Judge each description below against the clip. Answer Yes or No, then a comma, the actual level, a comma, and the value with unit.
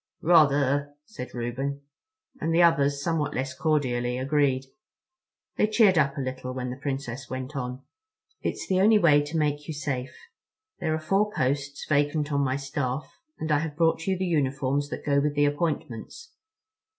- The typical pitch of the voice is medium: Yes, medium, 145 Hz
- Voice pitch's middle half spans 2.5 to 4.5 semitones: Yes, average, 2.9 semitones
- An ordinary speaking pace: Yes, average, 170 wpm